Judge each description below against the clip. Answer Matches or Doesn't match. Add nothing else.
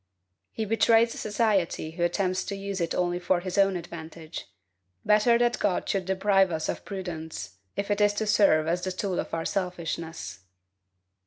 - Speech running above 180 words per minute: Doesn't match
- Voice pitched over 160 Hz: Matches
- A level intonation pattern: Doesn't match